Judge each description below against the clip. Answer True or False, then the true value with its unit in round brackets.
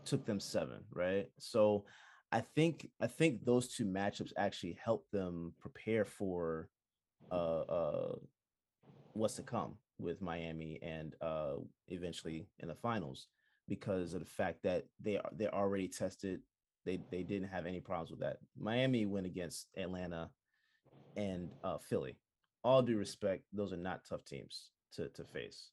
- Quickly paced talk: False (150 wpm)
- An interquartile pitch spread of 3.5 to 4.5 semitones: False (3.1 semitones)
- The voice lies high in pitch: False (95 Hz)